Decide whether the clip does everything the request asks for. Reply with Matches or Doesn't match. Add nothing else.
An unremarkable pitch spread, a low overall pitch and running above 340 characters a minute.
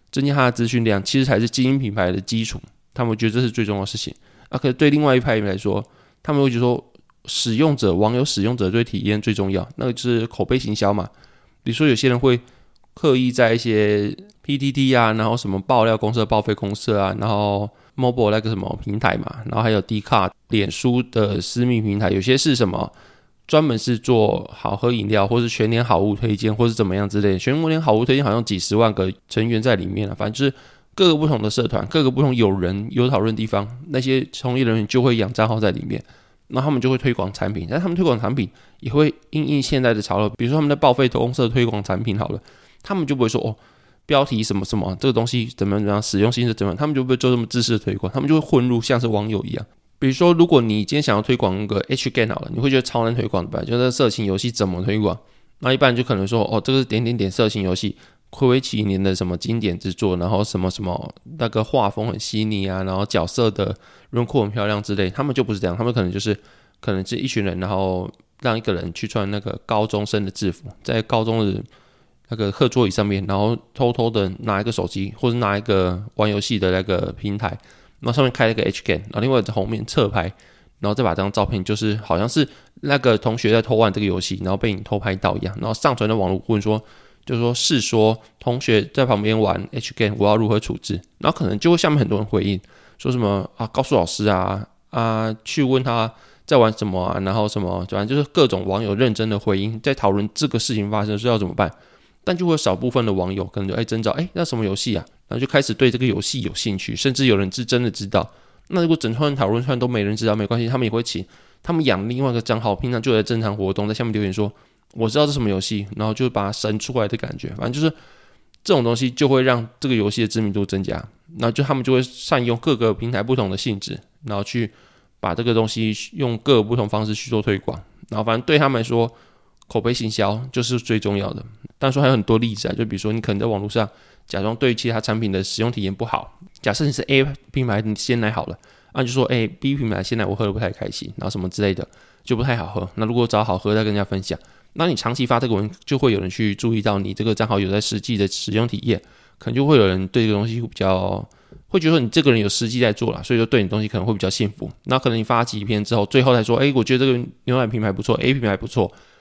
Matches